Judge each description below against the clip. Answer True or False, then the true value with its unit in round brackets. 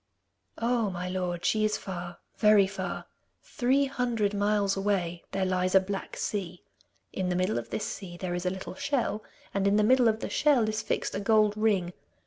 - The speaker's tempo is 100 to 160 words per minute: False (195 wpm)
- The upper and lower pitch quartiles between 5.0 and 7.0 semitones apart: False (2.9 semitones)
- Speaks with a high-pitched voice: True (200 Hz)